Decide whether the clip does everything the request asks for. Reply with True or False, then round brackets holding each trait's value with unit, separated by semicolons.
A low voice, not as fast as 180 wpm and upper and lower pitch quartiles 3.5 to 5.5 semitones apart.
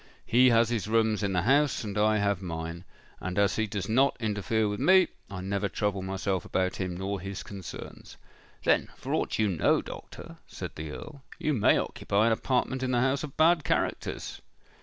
False (105 Hz; 195 wpm; 3.9 semitones)